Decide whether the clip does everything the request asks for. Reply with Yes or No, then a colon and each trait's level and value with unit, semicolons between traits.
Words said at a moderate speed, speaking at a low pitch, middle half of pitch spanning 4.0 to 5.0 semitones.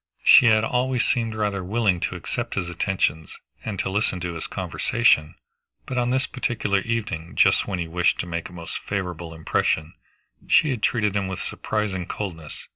Yes: average, 180 wpm; very low, 95 Hz; average, 4.4 semitones